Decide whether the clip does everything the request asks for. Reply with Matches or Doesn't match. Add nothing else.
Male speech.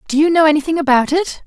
Doesn't match